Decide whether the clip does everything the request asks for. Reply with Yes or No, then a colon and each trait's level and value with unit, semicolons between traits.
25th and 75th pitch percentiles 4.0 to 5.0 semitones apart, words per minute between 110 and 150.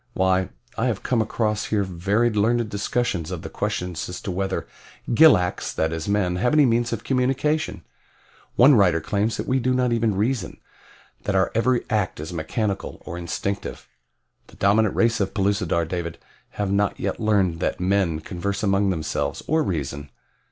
No: average, 4.4 semitones; average, 170 wpm